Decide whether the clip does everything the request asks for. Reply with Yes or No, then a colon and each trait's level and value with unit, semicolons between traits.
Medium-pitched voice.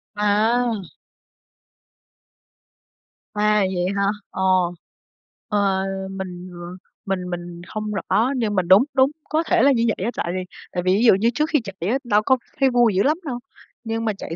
No: high, 210 Hz